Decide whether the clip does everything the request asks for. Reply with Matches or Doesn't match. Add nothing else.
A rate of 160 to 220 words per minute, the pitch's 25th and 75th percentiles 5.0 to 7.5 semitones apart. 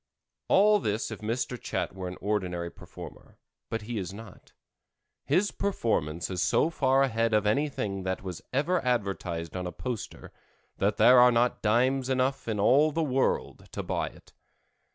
Matches